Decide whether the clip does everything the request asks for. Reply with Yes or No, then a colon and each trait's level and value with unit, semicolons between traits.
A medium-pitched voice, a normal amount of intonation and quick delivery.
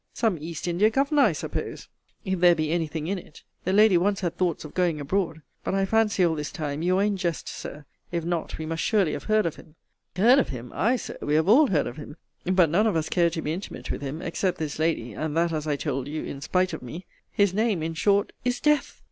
Yes: medium, 170 Hz; average, 4.2 semitones; fast, 255 wpm